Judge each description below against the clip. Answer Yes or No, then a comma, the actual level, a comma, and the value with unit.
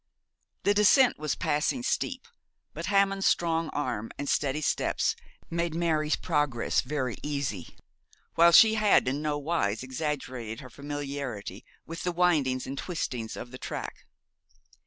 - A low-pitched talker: No, medium, 150 Hz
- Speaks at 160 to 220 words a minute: No, slow, 135 wpm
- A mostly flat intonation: No, average, 4.7 semitones